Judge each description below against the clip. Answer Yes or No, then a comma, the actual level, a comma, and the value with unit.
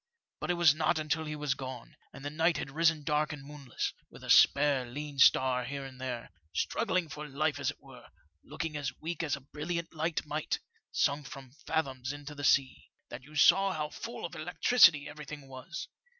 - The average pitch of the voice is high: No, medium, 150 Hz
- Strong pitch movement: No, average, 2.7 semitones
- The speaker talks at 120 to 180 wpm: No, average, 195 wpm